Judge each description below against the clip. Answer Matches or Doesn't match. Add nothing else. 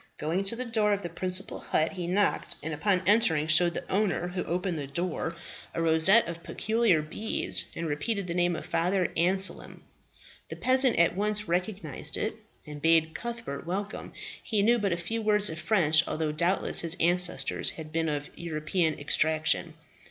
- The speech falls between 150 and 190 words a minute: Matches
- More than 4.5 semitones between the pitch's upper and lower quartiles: Doesn't match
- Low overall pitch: Doesn't match